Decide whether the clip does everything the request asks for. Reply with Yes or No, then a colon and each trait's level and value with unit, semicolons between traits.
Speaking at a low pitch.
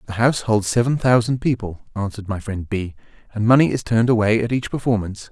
Yes: low, 110 Hz